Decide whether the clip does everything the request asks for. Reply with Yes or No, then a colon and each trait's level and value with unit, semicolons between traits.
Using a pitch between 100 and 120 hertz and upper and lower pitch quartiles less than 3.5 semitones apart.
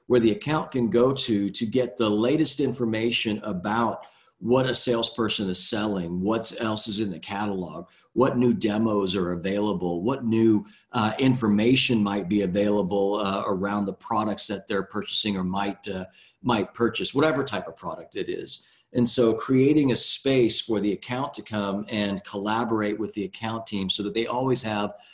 Yes: low, 110 Hz; average, 3.0 semitones